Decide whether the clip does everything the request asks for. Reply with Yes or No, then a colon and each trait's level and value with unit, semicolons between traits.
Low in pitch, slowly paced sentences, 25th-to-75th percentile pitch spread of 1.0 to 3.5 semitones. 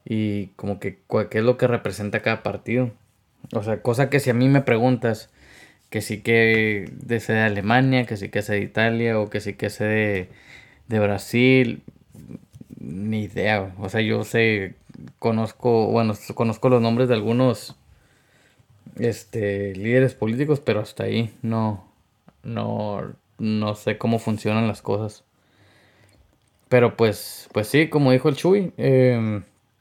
No: low, 110 Hz; average, 155 wpm; narrow, 2.6 semitones